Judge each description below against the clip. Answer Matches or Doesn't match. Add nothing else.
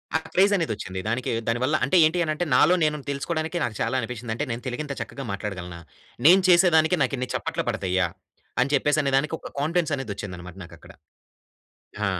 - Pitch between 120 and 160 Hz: Matches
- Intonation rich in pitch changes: Matches